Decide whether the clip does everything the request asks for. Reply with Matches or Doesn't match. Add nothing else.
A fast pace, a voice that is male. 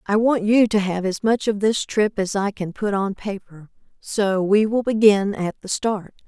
Doesn't match